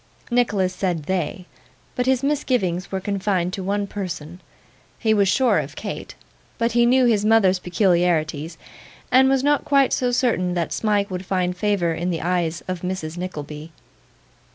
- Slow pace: No, average, 160 wpm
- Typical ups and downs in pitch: Yes, average, 4.3 semitones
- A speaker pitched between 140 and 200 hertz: Yes, high, 190 Hz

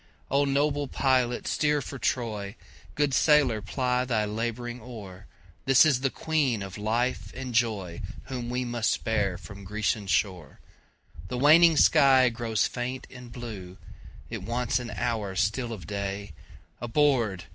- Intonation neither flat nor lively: Yes, average, 4.2 semitones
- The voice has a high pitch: No, low, 120 Hz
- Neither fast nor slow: No, slow, 125 wpm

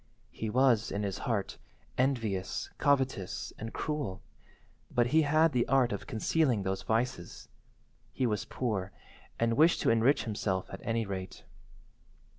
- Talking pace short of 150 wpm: Yes, average, 140 wpm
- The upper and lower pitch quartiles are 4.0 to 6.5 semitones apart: Yes, average, 4.7 semitones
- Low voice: Yes, low, 115 Hz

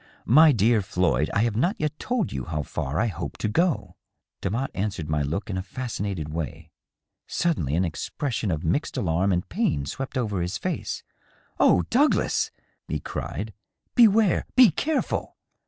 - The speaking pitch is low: Yes, low, 100 Hz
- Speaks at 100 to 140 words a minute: No, average, 175 wpm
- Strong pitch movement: Yes, wide, 8.8 semitones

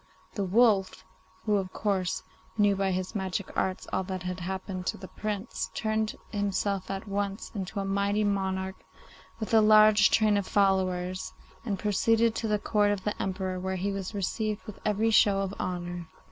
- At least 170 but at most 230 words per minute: Yes, average, 175 wpm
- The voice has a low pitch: No, high, 195 Hz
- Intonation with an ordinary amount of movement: No, narrow, 1.9 semitones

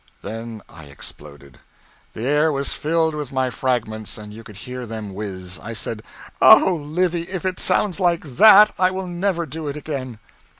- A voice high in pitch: No, low, 135 Hz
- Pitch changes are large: Yes, wide, 7.8 semitones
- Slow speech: No, average, 175 wpm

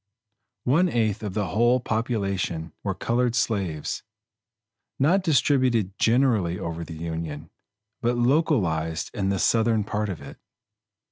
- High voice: No, low, 110 Hz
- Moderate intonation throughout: No, wide, 6.3 semitones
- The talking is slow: Yes, slow, 125 wpm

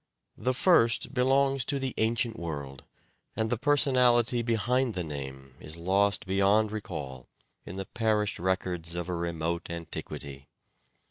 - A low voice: Yes, low, 100 Hz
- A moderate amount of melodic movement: No, wide, 6.1 semitones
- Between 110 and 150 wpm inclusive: Yes, slow, 135 wpm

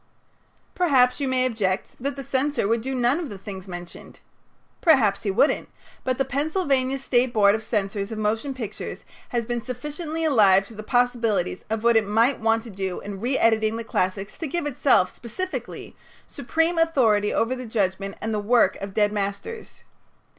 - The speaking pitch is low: No, high, 230 Hz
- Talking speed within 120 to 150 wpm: No, average, 175 wpm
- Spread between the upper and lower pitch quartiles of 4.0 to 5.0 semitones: Yes, average, 4.6 semitones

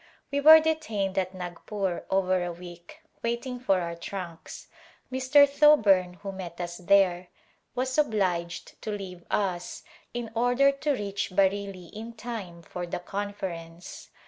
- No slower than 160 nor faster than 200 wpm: No, average, 140 wpm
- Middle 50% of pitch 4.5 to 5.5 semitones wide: Yes, average, 5.0 semitones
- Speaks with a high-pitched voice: Yes, high, 195 Hz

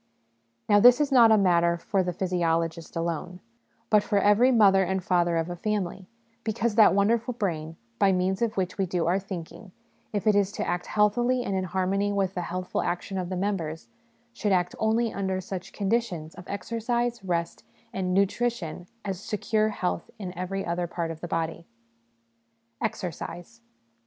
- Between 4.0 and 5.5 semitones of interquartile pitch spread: No, average, 3.2 semitones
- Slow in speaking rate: No, average, 170 wpm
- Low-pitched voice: No, high, 190 Hz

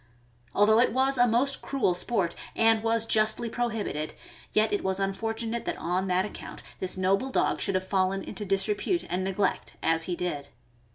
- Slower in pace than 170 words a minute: No, average, 175 wpm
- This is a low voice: No, high, 205 Hz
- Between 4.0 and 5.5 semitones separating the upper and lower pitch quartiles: No, average, 3.4 semitones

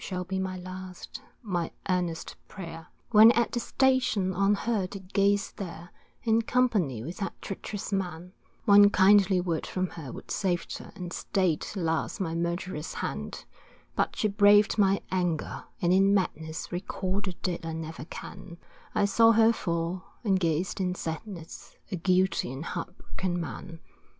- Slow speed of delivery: No, average, 155 wpm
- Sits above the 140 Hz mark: Yes, medium, 185 Hz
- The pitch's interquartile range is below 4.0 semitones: Yes, average, 2.9 semitones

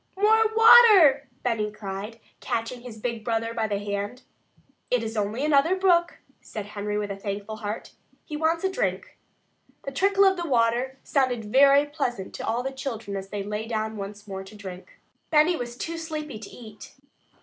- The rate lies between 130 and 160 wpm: No, average, 175 wpm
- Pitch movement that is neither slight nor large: No, wide, 6.3 semitones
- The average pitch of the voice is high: Yes, high, 235 Hz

